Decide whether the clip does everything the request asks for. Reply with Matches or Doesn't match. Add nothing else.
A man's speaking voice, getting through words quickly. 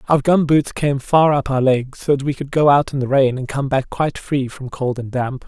Matches